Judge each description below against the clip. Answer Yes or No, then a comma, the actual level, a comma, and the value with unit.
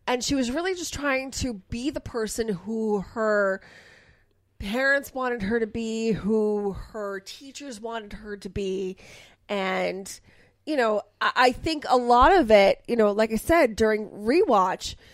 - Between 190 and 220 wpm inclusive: No, average, 165 wpm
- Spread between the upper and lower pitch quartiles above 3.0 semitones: Yes, average, 3.8 semitones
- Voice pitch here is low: No, high, 225 Hz